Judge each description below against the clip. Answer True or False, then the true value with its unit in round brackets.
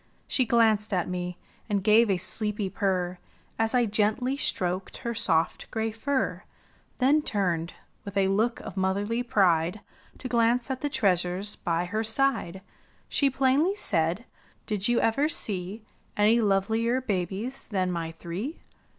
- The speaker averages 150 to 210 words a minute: False (140 wpm)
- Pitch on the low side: False (210 Hz)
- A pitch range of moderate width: True (4.3 semitones)